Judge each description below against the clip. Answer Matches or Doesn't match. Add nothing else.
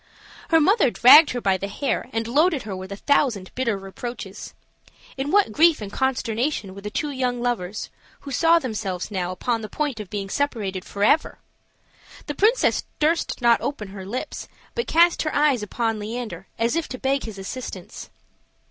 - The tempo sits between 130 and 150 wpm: Doesn't match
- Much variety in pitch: Matches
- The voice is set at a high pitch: Matches